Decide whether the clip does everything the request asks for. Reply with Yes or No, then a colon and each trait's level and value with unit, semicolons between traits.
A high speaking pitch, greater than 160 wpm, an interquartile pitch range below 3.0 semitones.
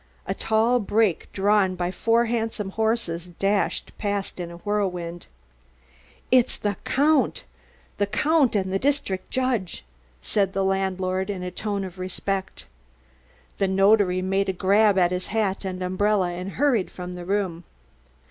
No: high, 195 Hz; average, 150 wpm; narrow, 2.6 semitones